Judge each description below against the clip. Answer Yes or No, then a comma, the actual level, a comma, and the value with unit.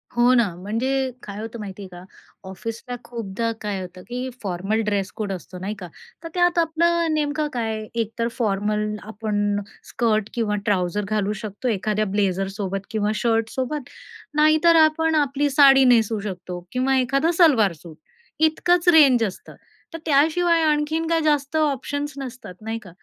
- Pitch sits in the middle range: No, high, 230 Hz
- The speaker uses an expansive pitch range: Yes, wide, 6.1 semitones